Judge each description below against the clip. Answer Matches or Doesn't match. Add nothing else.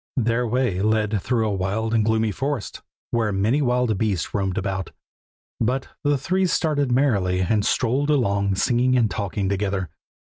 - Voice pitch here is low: Matches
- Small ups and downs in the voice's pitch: Doesn't match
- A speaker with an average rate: Matches